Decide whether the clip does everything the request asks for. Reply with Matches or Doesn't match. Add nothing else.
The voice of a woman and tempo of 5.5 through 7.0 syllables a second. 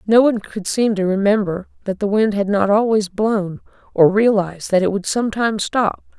Doesn't match